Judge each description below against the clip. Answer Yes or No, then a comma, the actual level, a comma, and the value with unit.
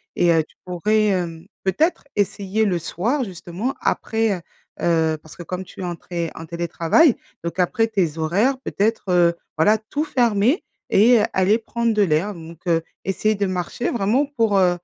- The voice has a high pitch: Yes, high, 195 Hz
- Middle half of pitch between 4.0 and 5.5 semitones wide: Yes, average, 4.5 semitones